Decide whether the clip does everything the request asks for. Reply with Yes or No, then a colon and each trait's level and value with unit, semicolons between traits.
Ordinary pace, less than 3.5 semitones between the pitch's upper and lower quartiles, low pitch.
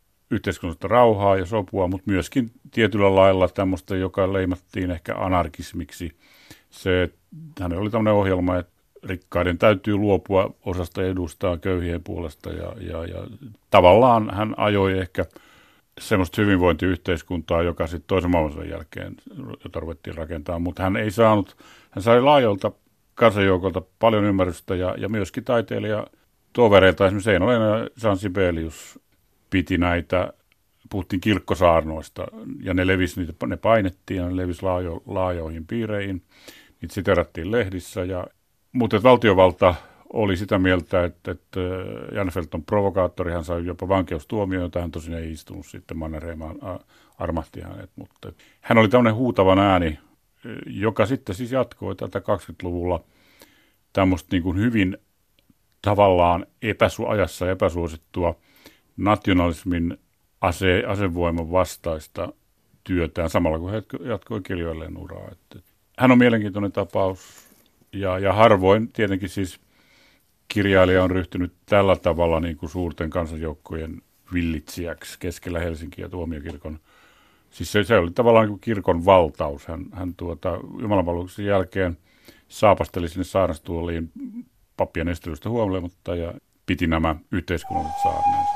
Yes: average, 120 wpm; average, 2.9 semitones; very low, 95 Hz